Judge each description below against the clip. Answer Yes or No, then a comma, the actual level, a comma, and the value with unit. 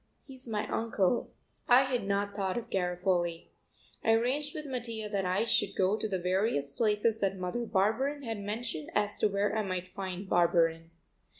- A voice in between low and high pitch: No, high, 205 Hz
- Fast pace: No, average, 175 wpm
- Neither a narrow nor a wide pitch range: Yes, average, 3.7 semitones